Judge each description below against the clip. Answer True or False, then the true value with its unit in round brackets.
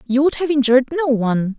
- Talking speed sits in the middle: False (225 wpm)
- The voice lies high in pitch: True (265 Hz)